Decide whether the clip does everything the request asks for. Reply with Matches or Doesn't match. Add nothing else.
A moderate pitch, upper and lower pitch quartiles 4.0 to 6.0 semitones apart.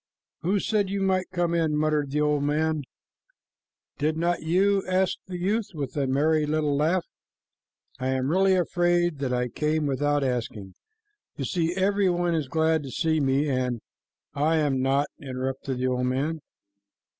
Matches